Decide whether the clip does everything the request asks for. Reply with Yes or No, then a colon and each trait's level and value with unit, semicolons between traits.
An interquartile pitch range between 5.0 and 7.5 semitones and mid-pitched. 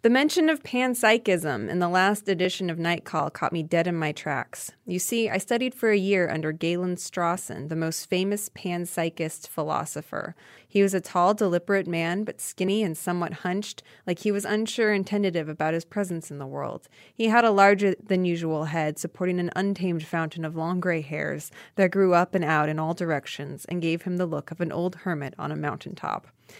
No: average, 3.2 semitones; medium, 180 Hz